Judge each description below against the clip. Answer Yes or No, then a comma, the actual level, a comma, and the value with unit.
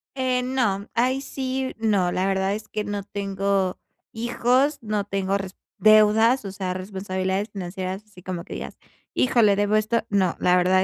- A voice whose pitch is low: No, high, 205 Hz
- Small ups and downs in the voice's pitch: No, average, 3.1 semitones